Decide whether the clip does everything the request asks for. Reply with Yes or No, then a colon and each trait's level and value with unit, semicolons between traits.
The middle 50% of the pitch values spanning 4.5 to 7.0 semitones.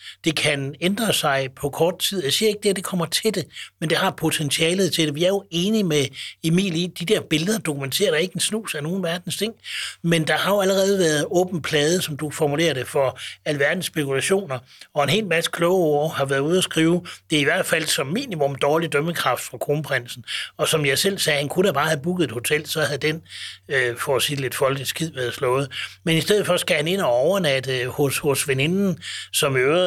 No: average, 4.1 semitones